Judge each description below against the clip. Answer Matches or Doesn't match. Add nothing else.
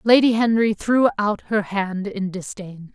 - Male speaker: Doesn't match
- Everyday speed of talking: Matches